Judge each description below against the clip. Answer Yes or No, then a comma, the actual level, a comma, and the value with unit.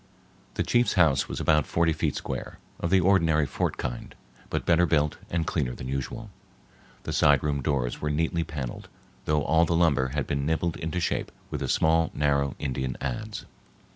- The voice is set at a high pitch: No, very low, 75 Hz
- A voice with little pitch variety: No, average, 3.2 semitones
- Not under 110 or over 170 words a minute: No, average, 180 wpm